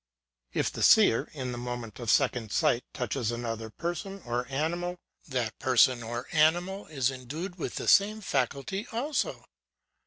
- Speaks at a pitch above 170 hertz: No, low, 135 Hz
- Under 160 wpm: Yes, average, 150 wpm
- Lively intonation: Yes, wide, 6.5 semitones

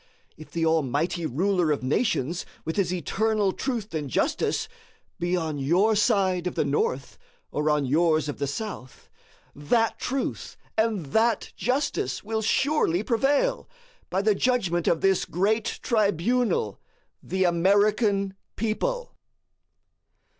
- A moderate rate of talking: No, slow, 125 wpm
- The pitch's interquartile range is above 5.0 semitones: Yes, wide, 5.5 semitones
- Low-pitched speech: No, high, 190 Hz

